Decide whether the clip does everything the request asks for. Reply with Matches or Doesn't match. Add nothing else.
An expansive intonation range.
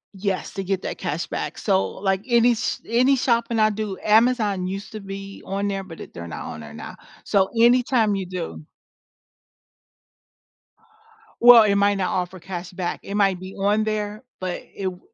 Doesn't match